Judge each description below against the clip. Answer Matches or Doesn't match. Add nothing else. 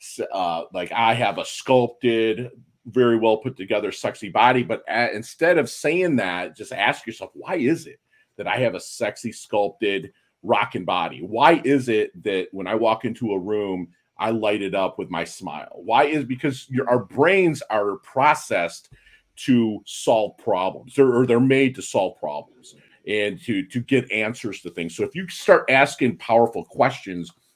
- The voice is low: Matches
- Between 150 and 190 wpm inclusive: Matches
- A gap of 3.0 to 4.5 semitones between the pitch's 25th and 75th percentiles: Matches